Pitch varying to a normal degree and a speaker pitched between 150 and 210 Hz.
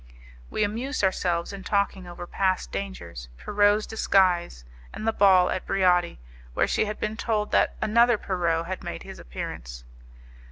Yes: average, 3.2 semitones; high, 190 Hz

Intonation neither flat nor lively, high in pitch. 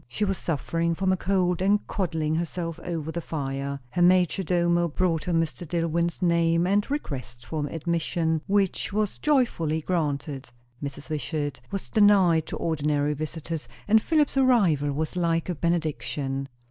No: average, 3.3 semitones; medium, 165 Hz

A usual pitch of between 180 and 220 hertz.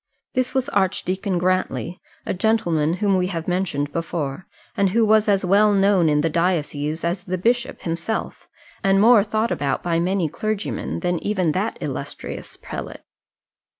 Yes: medium, 185 Hz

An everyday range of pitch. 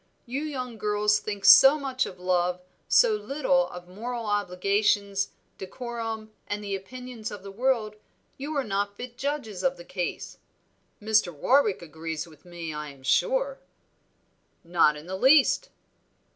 No: wide, 6.0 semitones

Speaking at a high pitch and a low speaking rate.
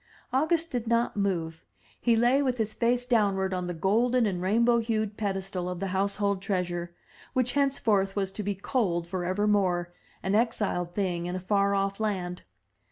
No: high, 200 Hz; average, 170 wpm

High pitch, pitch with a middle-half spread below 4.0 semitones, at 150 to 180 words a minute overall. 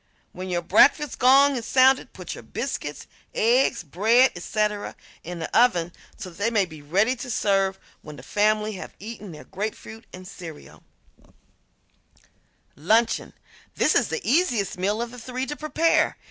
No: high, 215 Hz; average, 5.2 semitones; average, 160 wpm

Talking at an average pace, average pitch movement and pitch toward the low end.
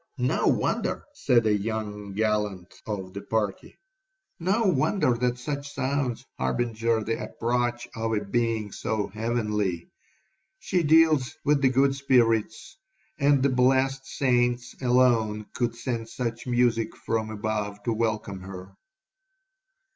No: slow, 125 wpm; average, 3.4 semitones; low, 115 Hz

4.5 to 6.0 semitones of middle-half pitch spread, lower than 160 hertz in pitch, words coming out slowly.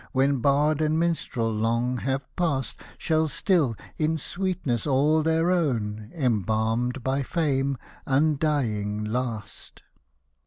Yes: average, 5.1 semitones; low, 135 Hz; slow, 110 wpm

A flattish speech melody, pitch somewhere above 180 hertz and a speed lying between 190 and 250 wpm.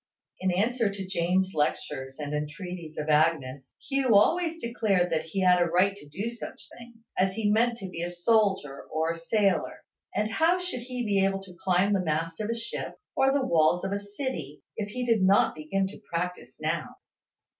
No: average, 5.2 semitones; high, 190 Hz; average, 200 wpm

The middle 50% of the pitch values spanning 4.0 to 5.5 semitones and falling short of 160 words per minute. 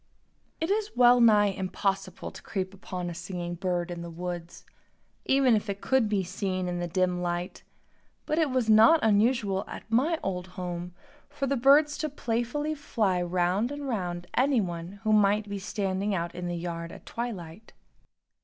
No: average, 5.2 semitones; average, 170 wpm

